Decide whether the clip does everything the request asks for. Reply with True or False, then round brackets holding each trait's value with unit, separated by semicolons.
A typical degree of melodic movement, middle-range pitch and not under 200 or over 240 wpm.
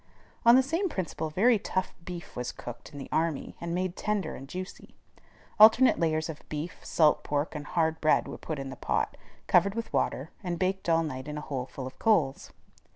True (4.1 semitones; 165 Hz; 205 wpm)